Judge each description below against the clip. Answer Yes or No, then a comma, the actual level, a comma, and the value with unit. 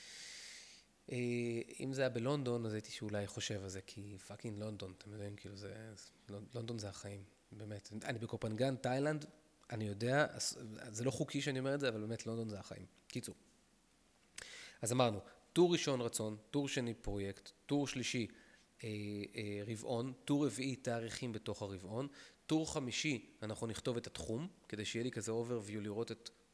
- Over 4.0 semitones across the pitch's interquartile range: No, average, 3.5 semitones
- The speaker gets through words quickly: Yes, fast, 160 wpm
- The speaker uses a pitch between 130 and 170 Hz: No, low, 115 Hz